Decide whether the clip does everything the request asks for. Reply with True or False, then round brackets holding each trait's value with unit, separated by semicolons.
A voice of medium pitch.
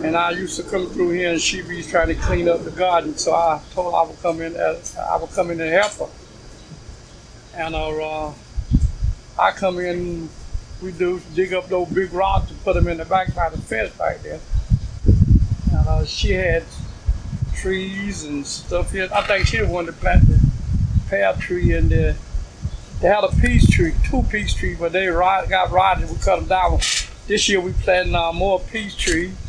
True (170 Hz)